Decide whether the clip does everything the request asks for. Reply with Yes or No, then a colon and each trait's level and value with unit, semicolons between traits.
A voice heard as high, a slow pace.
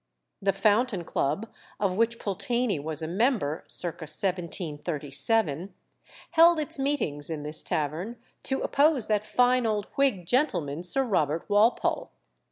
Yes: high, 200 Hz; slow, 130 wpm